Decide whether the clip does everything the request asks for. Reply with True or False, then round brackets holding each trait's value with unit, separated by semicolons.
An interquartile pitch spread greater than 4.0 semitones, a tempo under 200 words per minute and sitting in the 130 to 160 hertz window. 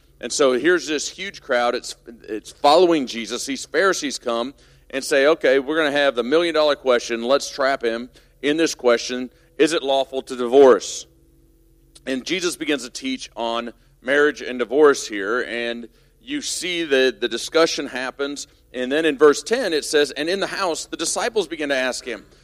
True (5.2 semitones; 185 wpm; 140 Hz)